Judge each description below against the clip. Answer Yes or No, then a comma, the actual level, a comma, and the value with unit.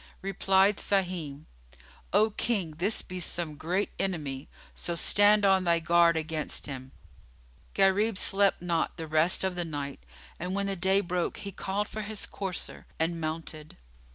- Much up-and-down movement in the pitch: No, average, 3.4 semitones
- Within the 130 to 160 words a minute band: Yes, average, 155 wpm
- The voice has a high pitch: No, medium, 180 Hz